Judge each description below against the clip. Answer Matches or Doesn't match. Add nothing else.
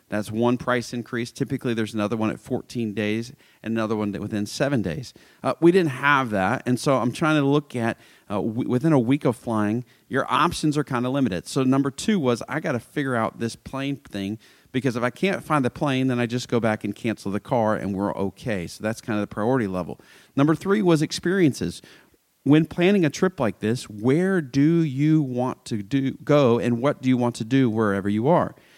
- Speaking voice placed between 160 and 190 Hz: Doesn't match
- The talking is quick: Matches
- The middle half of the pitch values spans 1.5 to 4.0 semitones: Doesn't match